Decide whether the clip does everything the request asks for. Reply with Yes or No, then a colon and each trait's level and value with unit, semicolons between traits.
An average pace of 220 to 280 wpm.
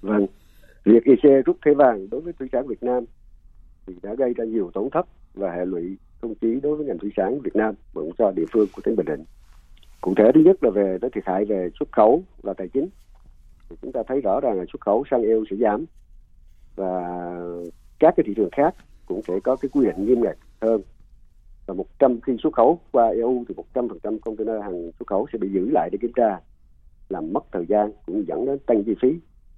Yes: average, 225 wpm